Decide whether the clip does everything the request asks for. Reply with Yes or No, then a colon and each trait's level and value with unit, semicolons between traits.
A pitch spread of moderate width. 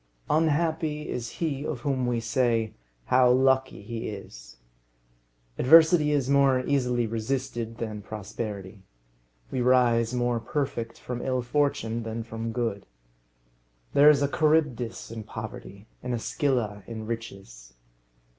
Yes: average, 3.5 semitones